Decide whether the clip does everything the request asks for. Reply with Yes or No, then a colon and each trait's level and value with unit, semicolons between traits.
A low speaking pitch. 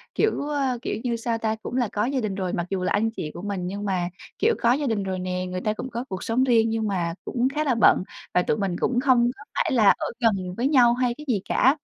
No: high, 225 Hz